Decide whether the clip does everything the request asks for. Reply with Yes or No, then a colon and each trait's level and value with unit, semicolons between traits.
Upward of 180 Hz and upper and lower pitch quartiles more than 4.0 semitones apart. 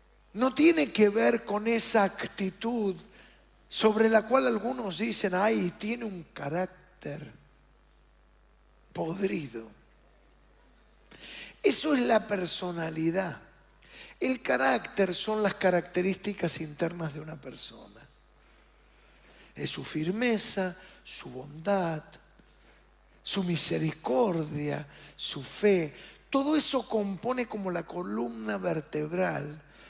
Yes: high, 190 Hz; average, 5.2 semitones